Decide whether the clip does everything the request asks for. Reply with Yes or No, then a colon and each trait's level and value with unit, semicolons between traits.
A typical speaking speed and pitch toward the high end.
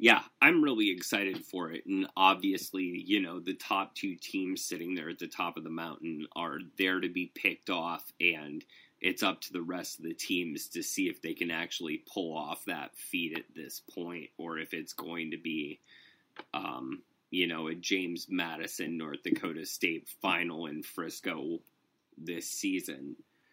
Yes: average, 180 wpm; very high, 295 Hz